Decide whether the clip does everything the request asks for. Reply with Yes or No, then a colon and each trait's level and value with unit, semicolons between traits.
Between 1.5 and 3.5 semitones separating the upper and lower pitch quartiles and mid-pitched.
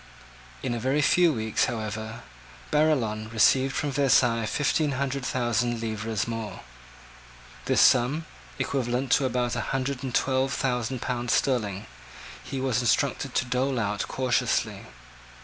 No: average, 2.8 semitones; low, 125 Hz